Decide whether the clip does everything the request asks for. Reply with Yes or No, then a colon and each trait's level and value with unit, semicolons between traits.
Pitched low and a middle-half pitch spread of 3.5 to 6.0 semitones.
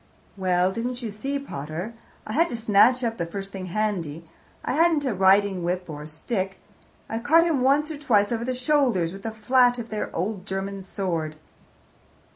No: high, 210 Hz; average, 5.2 semitones